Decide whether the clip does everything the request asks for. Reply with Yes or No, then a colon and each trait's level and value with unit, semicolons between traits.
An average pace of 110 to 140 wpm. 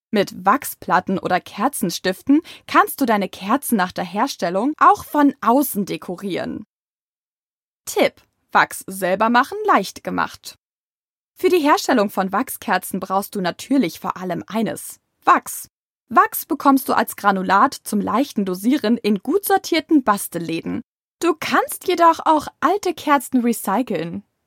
Yes: average, 130 wpm